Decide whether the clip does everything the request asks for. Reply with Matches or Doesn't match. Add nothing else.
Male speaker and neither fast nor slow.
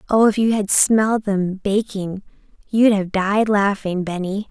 Doesn't match